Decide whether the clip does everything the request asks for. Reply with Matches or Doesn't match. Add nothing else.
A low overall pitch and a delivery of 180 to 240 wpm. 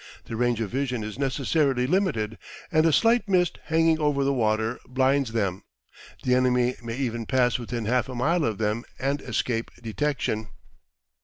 Doesn't match